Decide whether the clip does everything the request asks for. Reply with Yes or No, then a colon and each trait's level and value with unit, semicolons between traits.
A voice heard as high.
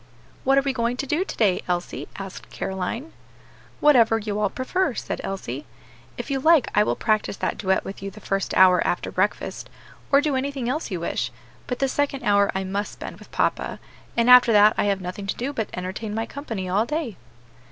Yes: high, 215 Hz